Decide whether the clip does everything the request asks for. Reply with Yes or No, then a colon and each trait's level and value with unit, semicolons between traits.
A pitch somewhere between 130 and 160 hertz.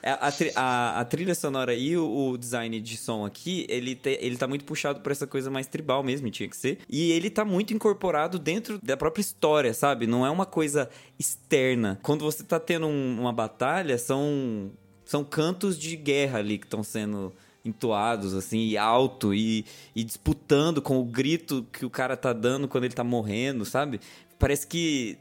Yes: low, 135 Hz